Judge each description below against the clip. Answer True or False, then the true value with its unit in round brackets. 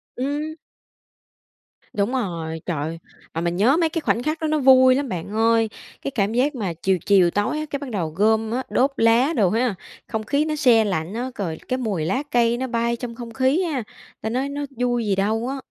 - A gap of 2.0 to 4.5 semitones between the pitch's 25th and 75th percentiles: False (4.9 semitones)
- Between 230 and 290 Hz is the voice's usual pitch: True (235 Hz)